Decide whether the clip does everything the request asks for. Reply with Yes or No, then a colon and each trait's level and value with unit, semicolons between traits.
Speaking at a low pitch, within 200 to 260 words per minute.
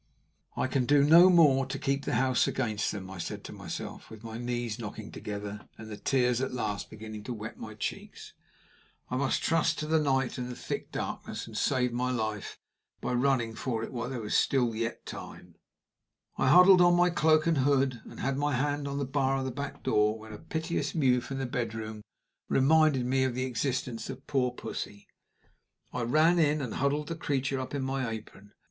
Yes: low, 130 Hz; fast, 205 wpm